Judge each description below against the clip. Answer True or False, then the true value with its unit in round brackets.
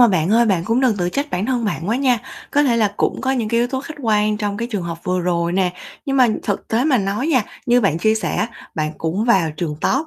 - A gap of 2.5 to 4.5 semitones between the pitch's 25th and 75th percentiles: False (5.1 semitones)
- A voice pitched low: False (215 Hz)